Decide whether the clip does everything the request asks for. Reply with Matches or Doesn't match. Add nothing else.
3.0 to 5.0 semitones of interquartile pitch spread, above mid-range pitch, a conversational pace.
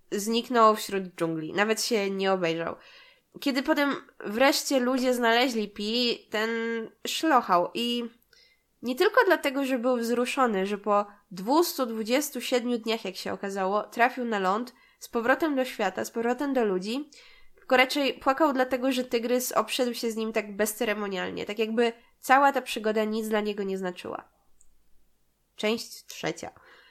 Matches